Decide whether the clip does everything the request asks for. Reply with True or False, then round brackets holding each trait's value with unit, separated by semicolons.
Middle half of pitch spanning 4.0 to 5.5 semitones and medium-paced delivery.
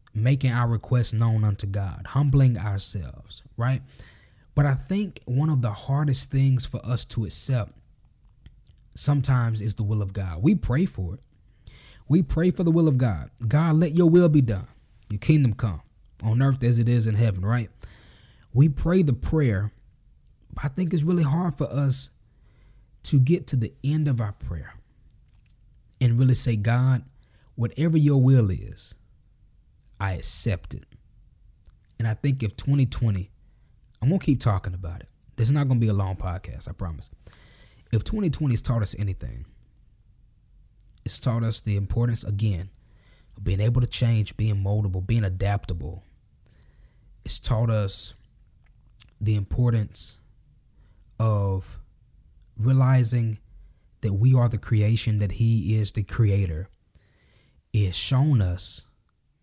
True (4.3 semitones; 150 wpm)